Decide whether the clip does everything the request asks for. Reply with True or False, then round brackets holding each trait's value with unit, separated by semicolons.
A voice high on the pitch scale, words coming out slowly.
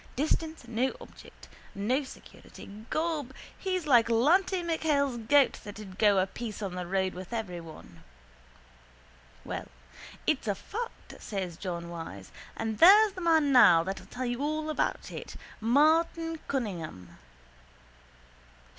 True (240 Hz; 130 wpm)